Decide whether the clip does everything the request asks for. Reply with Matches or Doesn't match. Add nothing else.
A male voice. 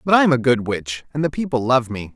Matches